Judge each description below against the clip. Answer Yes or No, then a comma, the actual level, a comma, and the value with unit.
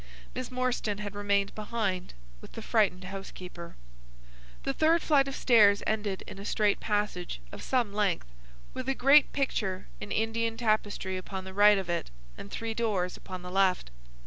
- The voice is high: Yes, high, 205 Hz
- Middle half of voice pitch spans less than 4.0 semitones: Yes, average, 3.4 semitones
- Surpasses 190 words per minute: No, average, 170 wpm